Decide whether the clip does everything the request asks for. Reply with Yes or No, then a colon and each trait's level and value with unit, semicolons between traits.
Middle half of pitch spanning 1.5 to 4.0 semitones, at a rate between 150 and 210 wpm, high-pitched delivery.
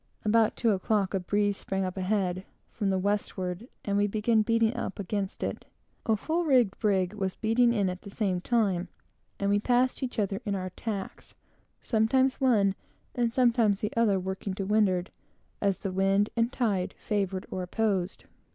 Yes: average, 3.0 semitones; average, 175 wpm; high, 205 Hz